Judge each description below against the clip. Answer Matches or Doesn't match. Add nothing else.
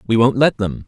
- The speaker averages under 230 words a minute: Doesn't match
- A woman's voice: Doesn't match